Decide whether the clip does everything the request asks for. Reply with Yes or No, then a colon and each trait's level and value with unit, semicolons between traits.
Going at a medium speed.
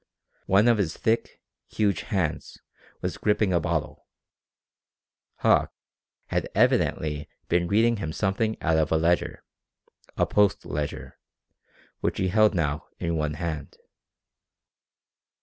No: slow, 120 wpm